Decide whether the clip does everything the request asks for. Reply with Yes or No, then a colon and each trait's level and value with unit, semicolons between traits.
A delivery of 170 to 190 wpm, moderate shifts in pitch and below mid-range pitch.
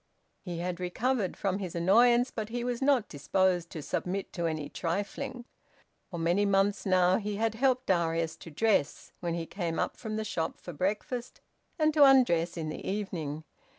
No: average, 180 wpm; average, 5.0 semitones; high, 190 Hz